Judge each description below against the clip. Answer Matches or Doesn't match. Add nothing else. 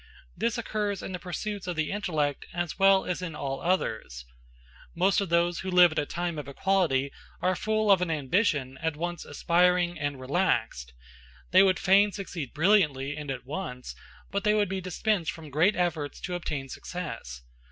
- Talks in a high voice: Doesn't match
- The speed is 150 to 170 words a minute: Doesn't match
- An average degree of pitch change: Matches